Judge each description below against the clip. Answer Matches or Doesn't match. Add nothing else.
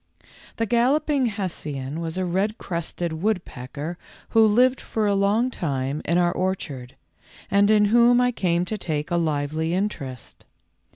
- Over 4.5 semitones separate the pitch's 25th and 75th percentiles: Matches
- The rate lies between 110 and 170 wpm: Matches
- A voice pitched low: Doesn't match